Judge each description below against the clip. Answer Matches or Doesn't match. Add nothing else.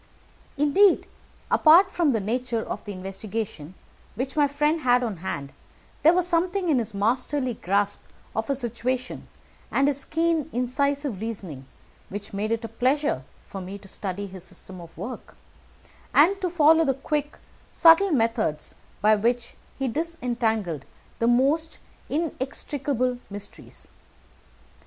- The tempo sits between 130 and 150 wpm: Matches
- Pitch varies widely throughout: Matches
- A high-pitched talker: Matches